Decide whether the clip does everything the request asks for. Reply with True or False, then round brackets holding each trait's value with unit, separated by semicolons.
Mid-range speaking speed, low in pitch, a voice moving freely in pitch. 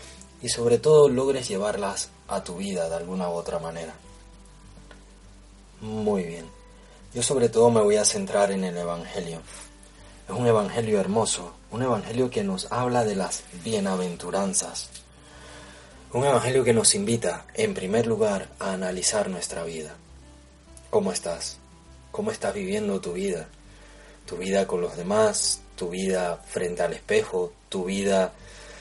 True (140 wpm; 100 Hz; 6.4 semitones)